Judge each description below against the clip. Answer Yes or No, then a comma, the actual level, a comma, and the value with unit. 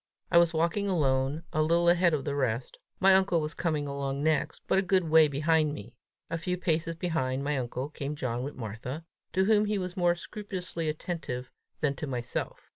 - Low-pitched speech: No, medium, 155 Hz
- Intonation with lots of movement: No, average, 4.1 semitones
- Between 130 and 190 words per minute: No, average, 200 wpm